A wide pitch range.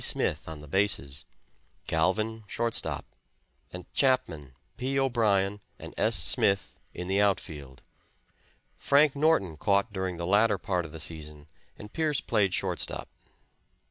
Yes: wide, 5.7 semitones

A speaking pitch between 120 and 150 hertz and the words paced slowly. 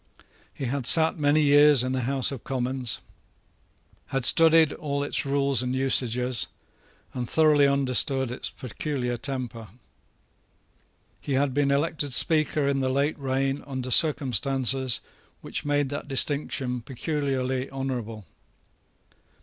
Yes: low, 135 Hz; slow, 125 wpm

